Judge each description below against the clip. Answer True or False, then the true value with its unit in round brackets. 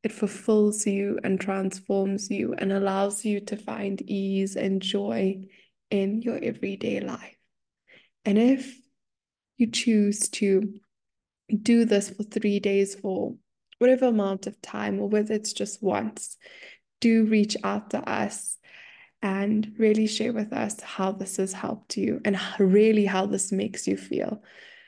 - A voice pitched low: False (210 Hz)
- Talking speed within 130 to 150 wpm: True (145 wpm)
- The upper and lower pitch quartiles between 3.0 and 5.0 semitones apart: False (2.4 semitones)